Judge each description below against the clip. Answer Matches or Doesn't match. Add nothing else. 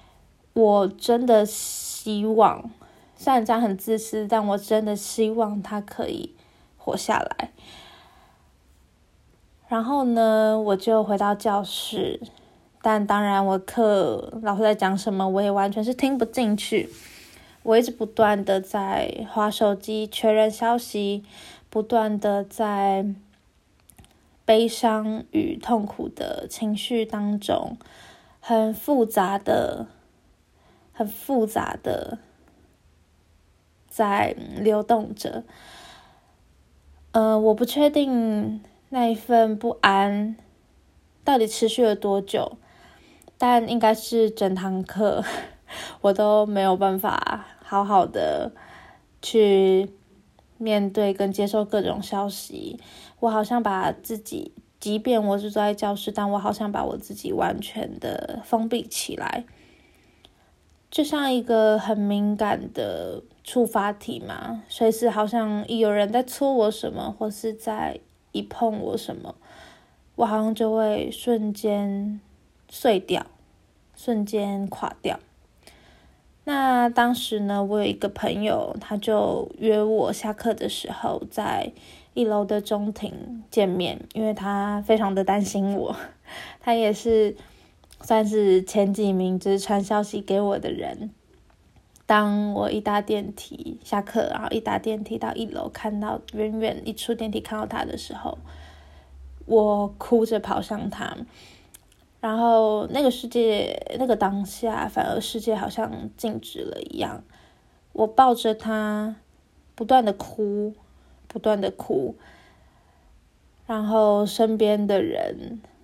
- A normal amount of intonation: Doesn't match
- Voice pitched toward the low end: Doesn't match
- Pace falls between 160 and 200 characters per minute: Matches